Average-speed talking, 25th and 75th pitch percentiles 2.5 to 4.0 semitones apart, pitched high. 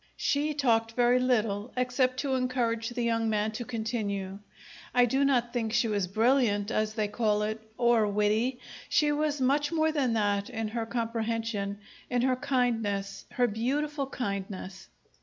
Yes: average, 160 wpm; average, 3.1 semitones; high, 230 Hz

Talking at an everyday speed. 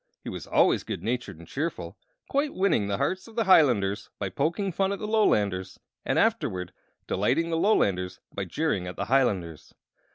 Yes: average, 175 wpm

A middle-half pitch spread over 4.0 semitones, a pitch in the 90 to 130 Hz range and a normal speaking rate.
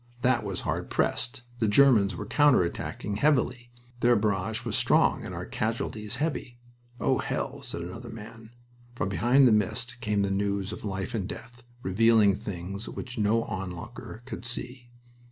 No: average, 3.3 semitones; low, 110 Hz; average, 160 wpm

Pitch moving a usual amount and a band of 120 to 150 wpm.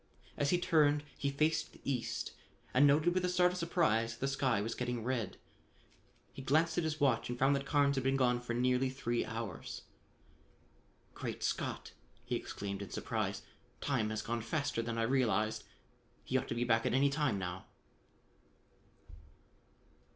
No: average, 3.9 semitones; average, 175 wpm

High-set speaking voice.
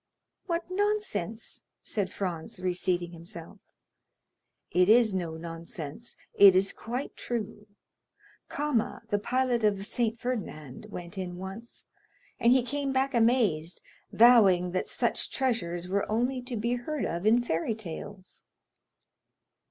Yes: high, 215 Hz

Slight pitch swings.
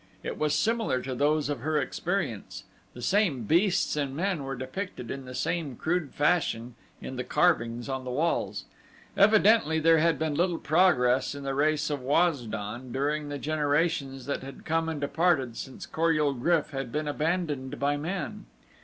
No: average, 3.8 semitones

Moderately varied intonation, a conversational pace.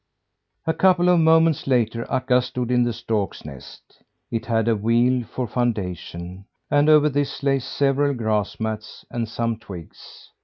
Yes: average, 4.0 semitones; average, 155 wpm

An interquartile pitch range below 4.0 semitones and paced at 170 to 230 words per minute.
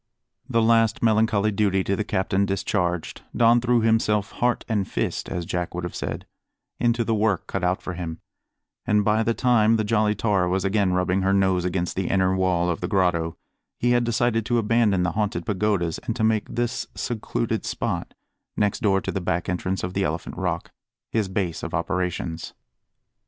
Yes: average, 3.5 semitones; average, 190 wpm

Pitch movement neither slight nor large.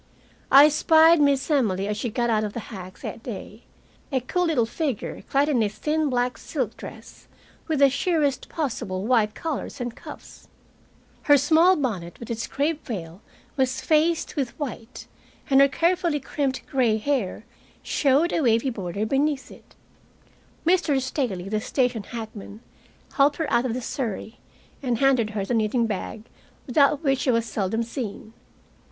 Yes: average, 4.7 semitones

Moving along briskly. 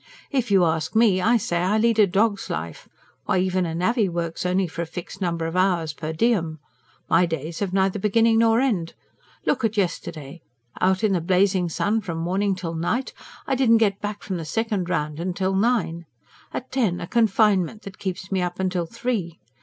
No: average, 195 wpm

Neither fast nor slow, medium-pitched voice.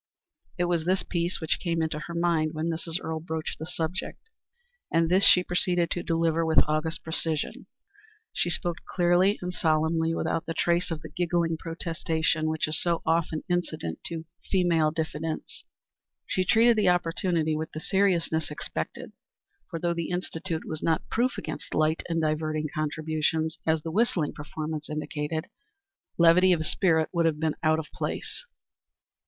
Yes: average, 160 wpm; medium, 165 Hz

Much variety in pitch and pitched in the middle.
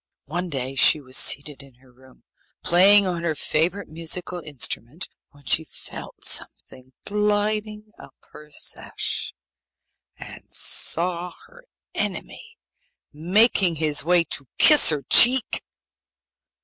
Yes: wide, 5.9 semitones; medium, 170 Hz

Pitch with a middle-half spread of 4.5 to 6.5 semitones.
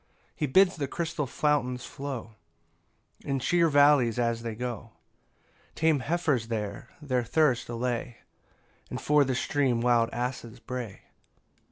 No: average, 3.8 semitones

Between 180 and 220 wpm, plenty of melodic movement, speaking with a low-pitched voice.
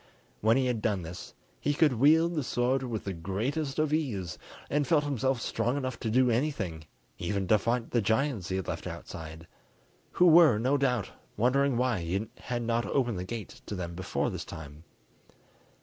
Yes: average, 185 wpm; wide, 6.0 semitones; low, 120 Hz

